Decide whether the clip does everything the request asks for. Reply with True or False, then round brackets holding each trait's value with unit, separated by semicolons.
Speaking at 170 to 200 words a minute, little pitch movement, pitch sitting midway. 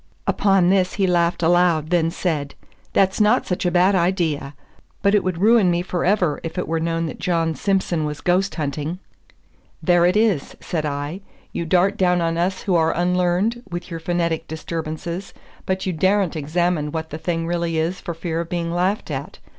True (185 wpm; 2.2 semitones; 175 Hz)